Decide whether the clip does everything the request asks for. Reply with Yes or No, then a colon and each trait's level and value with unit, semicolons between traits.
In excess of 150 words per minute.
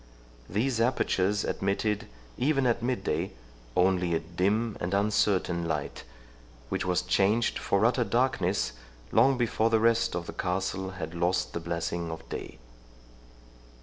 No: average, 140 wpm